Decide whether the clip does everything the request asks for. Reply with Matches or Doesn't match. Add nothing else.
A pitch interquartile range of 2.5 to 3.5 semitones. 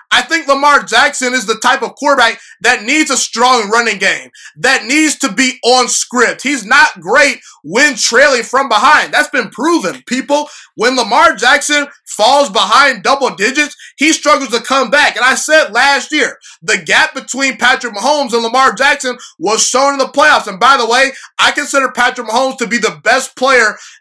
Matches